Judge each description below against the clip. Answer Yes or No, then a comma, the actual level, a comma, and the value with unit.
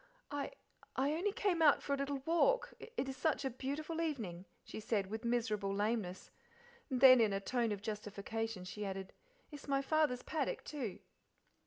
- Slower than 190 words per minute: Yes, average, 175 wpm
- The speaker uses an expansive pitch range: Yes, wide, 5.9 semitones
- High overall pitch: Yes, very high, 255 Hz